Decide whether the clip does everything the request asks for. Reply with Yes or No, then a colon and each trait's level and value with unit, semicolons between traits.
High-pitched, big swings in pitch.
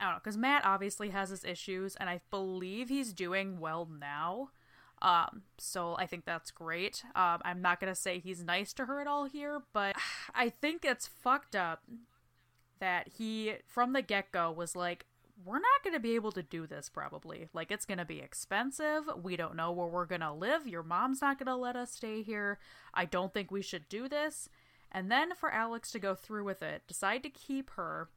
Yes: high, 200 Hz; wide, 6.1 semitones